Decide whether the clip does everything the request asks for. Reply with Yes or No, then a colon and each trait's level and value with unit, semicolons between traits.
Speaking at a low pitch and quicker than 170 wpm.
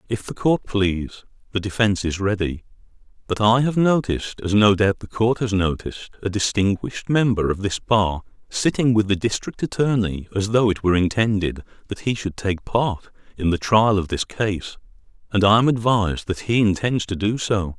Yes: low, 105 Hz; average, 190 wpm